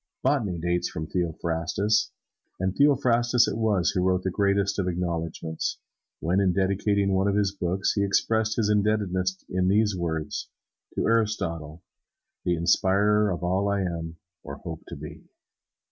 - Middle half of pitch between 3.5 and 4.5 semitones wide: No, average, 3.0 semitones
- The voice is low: Yes, very low, 95 Hz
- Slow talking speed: No, average, 150 wpm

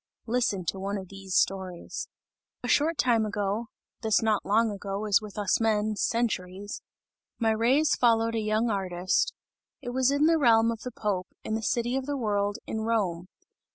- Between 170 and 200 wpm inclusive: Yes, average, 180 wpm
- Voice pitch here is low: No, high, 220 Hz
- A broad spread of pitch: No, average, 2.8 semitones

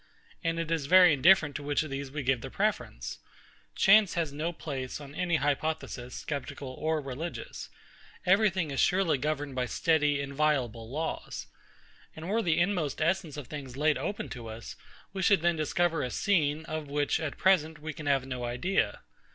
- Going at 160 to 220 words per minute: Yes, average, 180 wpm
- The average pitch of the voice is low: No, medium, 150 Hz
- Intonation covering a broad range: No, average, 3.4 semitones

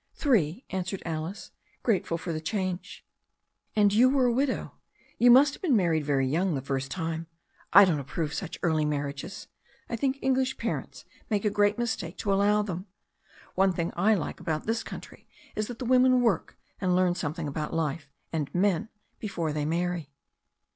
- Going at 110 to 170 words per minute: No, average, 180 wpm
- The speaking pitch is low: No, medium, 185 Hz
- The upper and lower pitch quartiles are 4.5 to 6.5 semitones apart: Yes, wide, 5.4 semitones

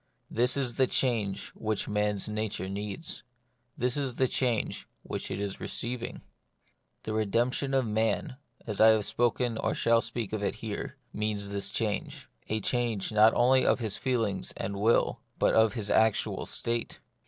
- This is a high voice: No, low, 110 Hz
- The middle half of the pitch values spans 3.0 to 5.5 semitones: No, narrow, 2.6 semitones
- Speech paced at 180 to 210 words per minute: No, average, 165 wpm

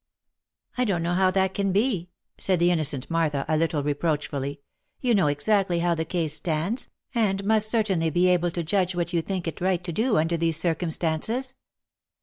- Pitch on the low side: No, medium, 175 Hz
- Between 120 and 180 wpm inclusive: No, average, 195 wpm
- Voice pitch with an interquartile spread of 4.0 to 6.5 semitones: No, average, 3.3 semitones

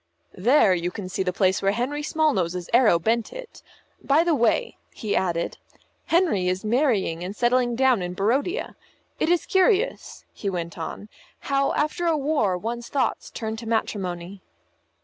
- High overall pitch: Yes, high, 225 Hz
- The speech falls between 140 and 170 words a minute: Yes, average, 160 wpm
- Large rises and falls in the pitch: Yes, wide, 7.7 semitones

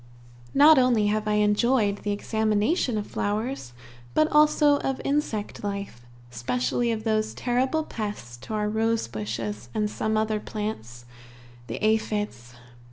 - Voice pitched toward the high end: Yes, high, 215 Hz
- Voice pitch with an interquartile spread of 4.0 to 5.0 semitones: No, average, 2.8 semitones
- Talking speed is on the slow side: Yes, slow, 130 wpm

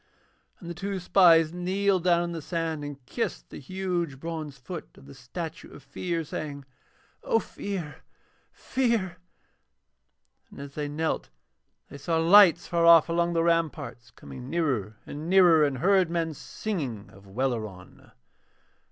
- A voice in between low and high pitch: Yes, medium, 165 Hz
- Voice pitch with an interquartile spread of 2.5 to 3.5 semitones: No, average, 4.0 semitones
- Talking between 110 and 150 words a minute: Yes, average, 145 wpm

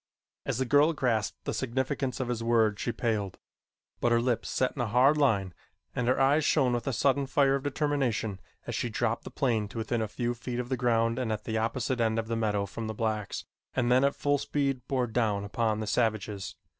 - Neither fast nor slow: No, fast, 225 wpm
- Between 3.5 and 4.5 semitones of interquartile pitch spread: No, average, 3.0 semitones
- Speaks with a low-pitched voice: Yes, low, 120 Hz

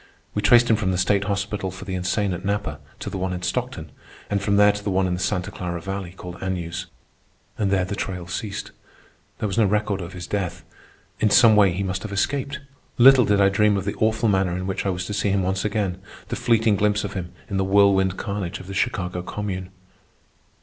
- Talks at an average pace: No, fast, 225 wpm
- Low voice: Yes, low, 100 Hz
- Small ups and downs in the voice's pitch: Yes, narrow, 2.0 semitones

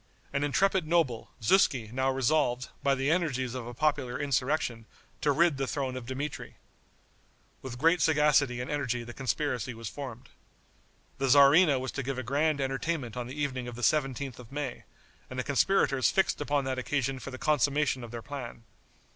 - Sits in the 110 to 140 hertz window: Yes, low, 135 Hz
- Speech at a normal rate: Yes, average, 180 wpm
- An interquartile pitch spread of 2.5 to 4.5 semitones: Yes, average, 2.8 semitones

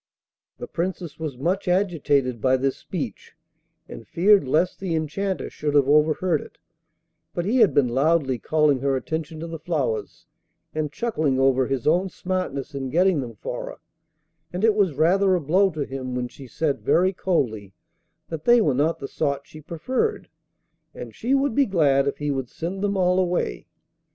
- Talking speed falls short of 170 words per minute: No, average, 180 wpm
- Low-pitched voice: No, medium, 155 Hz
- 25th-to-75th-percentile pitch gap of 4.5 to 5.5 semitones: Yes, average, 5.2 semitones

